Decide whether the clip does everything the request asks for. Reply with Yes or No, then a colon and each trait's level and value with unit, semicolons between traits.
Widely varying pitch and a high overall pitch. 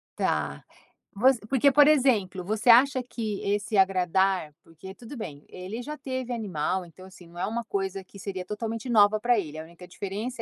No: average, 4.3 semitones; high, 205 Hz